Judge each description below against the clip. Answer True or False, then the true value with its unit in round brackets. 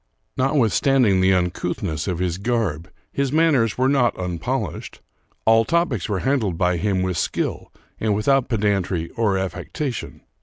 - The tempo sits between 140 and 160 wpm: True (145 wpm)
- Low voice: True (105 Hz)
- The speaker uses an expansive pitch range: True (5.9 semitones)